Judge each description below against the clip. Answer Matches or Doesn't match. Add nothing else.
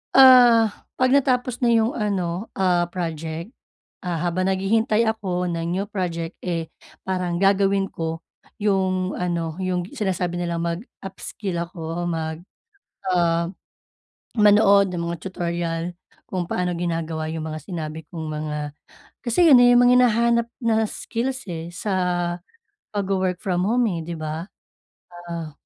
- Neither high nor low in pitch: Matches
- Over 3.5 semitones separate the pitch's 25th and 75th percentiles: Matches